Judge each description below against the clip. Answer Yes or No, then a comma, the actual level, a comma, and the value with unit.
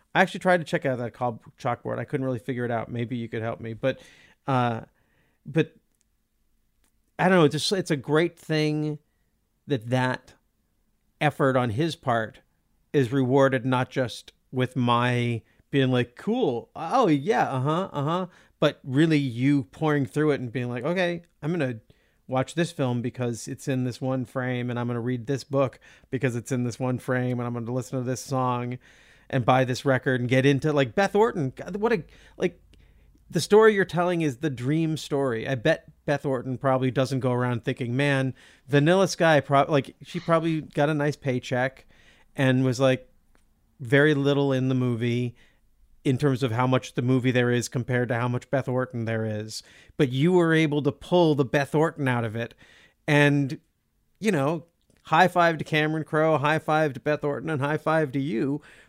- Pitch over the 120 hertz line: Yes, low, 135 Hz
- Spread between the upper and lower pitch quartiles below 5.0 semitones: Yes, average, 3.5 semitones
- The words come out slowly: No, average, 195 wpm